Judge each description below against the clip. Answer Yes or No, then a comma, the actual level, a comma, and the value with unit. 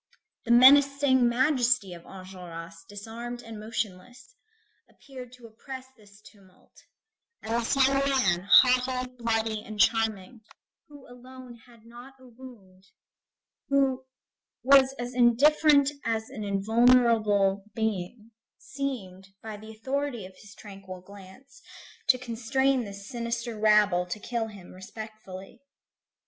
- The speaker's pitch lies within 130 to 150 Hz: No, high, 230 Hz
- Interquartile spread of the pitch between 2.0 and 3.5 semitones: No, average, 4.1 semitones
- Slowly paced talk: Yes, slow, 120 wpm